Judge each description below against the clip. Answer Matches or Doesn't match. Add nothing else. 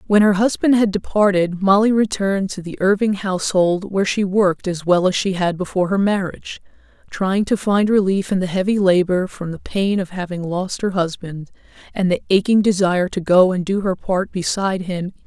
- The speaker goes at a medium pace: Doesn't match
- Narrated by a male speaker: Doesn't match